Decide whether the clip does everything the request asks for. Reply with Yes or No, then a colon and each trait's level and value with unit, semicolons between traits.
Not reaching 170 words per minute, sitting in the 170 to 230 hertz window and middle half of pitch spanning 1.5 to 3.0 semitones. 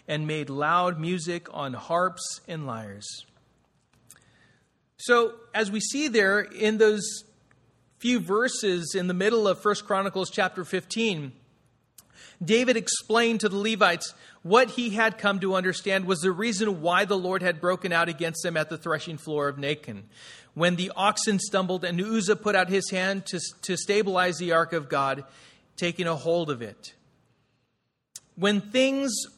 No: average, 155 wpm; medium, 185 Hz; average, 4.4 semitones